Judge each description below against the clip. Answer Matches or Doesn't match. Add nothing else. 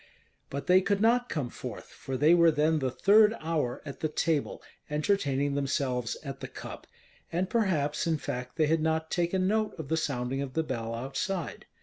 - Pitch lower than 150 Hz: Doesn't match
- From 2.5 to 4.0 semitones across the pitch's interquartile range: Doesn't match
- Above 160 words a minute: Matches